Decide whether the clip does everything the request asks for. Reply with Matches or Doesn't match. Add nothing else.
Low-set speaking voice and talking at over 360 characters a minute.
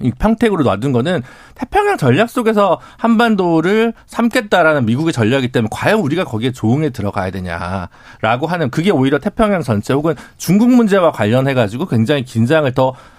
Doesn't match